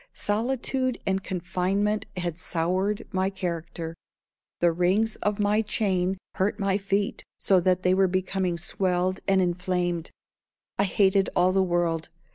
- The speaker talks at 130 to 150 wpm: Yes, slow, 135 wpm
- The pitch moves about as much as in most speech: No, narrow, 2.0 semitones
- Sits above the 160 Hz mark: Yes, medium, 185 Hz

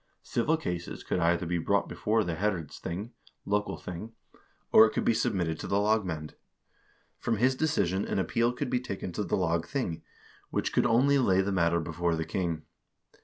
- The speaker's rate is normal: Yes, average, 175 wpm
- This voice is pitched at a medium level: No, very low, 95 Hz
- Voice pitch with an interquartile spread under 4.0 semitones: No, average, 5.1 semitones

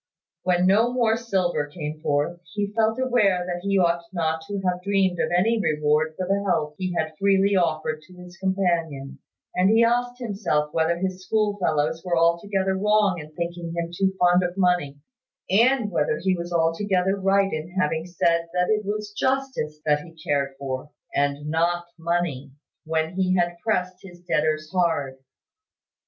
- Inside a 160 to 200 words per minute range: Yes, average, 170 wpm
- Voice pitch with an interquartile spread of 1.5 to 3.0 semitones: No, average, 3.6 semitones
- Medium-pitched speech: Yes, medium, 180 Hz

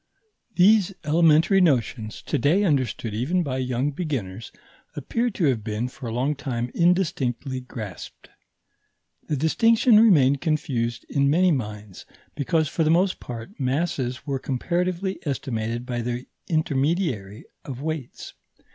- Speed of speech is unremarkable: No, slow, 130 wpm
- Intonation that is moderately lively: No, wide, 5.7 semitones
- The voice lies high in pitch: No, medium, 140 Hz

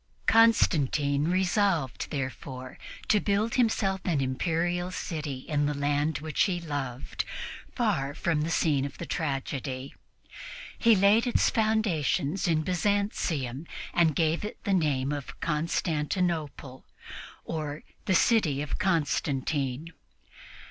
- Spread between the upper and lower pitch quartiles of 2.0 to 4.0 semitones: No, average, 4.8 semitones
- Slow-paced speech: Yes, slow, 115 wpm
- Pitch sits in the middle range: Yes, medium, 160 Hz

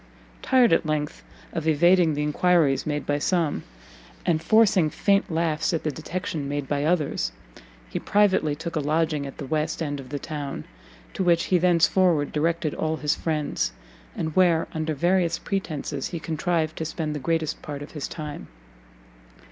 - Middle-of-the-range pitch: Yes, medium, 160 Hz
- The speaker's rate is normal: Yes, average, 170 wpm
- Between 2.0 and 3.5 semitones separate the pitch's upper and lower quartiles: Yes, narrow, 2.5 semitones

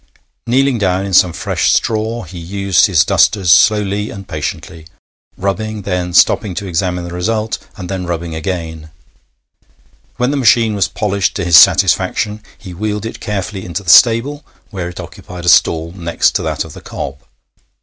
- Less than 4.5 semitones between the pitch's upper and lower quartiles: Yes, average, 3.5 semitones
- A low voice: Yes, very low, 95 Hz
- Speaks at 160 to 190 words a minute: Yes, average, 170 wpm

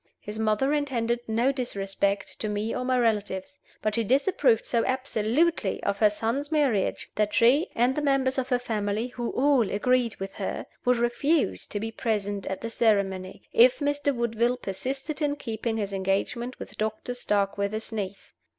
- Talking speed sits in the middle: Yes, average, 170 wpm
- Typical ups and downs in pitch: Yes, average, 3.9 semitones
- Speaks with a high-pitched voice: Yes, high, 230 Hz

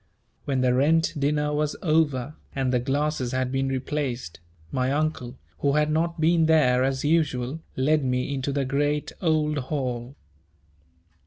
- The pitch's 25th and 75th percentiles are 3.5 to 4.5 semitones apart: No, average, 2.8 semitones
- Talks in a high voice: No, medium, 140 Hz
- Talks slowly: No, average, 150 wpm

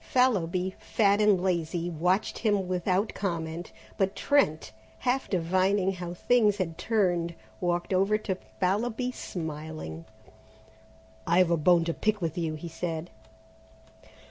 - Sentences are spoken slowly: Yes, slow, 125 wpm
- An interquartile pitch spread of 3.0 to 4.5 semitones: Yes, average, 3.4 semitones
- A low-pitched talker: No, medium, 180 Hz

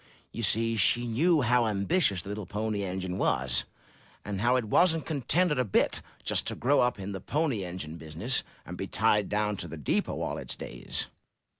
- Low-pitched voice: Yes, low, 105 Hz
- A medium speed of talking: Yes, average, 190 wpm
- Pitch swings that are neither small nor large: Yes, average, 4.7 semitones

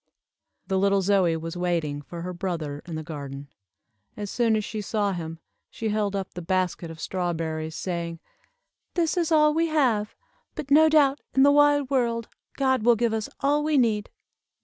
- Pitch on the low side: No, high, 205 Hz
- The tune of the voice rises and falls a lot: Yes, wide, 7.9 semitones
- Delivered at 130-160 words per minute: No, average, 180 wpm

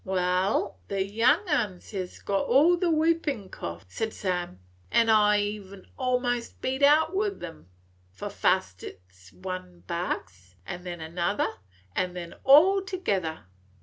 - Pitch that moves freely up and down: Yes, wide, 7.2 semitones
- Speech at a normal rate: Yes, average, 150 wpm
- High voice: Yes, high, 200 Hz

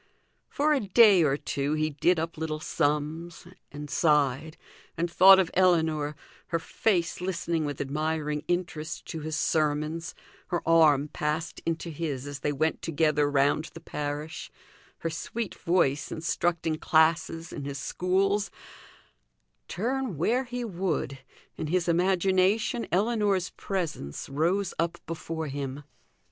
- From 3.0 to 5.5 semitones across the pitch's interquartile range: Yes, average, 3.4 semitones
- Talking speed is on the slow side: Yes, slow, 130 wpm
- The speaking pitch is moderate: Yes, medium, 165 Hz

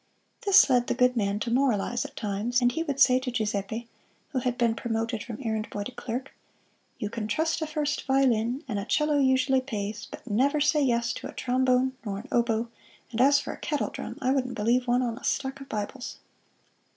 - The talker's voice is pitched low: No, high, 245 Hz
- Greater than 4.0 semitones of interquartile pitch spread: No, average, 3.0 semitones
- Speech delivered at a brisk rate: Yes, fast, 210 wpm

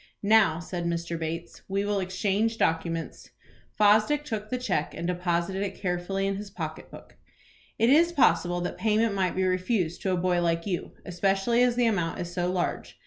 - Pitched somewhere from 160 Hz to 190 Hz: Yes, medium, 185 Hz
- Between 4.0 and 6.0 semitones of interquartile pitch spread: No, average, 3.3 semitones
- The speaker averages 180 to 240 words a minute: Yes, average, 185 wpm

